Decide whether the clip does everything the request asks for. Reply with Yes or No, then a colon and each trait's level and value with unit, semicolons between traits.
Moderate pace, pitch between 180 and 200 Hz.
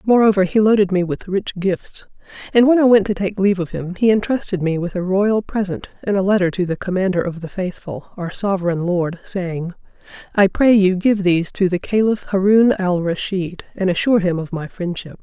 No: fast, 210 wpm; high, 190 Hz